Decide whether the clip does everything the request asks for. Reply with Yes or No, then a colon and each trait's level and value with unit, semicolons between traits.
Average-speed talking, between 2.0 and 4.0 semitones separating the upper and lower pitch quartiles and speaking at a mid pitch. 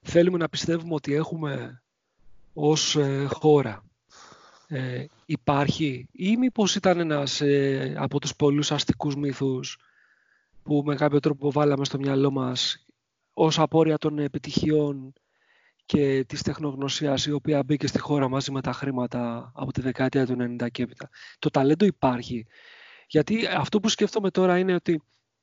Yes: average, 145 wpm; narrow, 2.5 semitones; medium, 145 Hz